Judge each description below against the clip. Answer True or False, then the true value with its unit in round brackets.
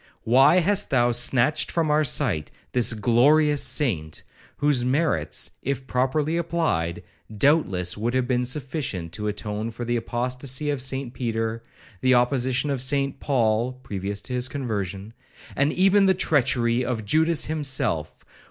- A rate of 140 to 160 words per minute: True (145 wpm)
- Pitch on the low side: True (125 Hz)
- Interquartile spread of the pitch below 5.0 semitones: True (4.3 semitones)